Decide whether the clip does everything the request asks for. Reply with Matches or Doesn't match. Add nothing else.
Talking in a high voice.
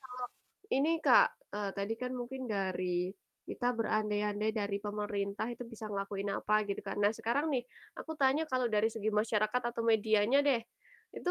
Matches